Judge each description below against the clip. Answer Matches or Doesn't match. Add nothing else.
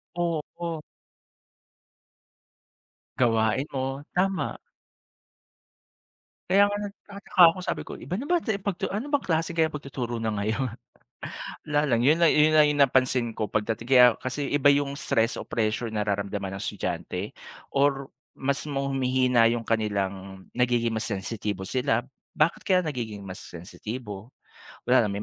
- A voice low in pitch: Matches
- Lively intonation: Matches